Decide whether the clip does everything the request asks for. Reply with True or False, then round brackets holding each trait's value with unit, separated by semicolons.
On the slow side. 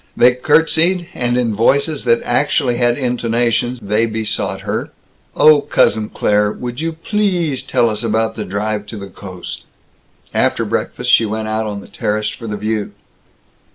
False (155 wpm)